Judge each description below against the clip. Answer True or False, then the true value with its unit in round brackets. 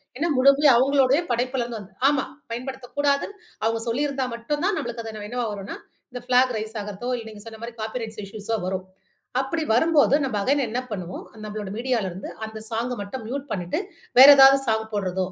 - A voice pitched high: True (240 Hz)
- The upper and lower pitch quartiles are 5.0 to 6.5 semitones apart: False (3.7 semitones)